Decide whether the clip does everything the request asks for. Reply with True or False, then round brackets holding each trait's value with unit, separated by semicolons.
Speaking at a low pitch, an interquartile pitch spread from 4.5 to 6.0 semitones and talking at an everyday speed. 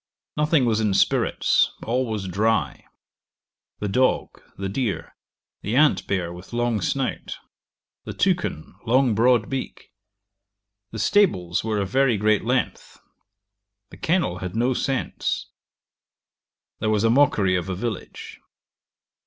False (110 Hz; 4.8 semitones; 130 wpm)